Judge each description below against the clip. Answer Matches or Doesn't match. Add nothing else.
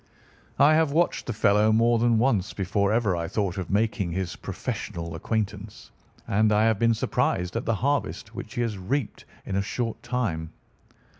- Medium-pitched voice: Doesn't match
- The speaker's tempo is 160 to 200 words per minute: Matches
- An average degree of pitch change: Matches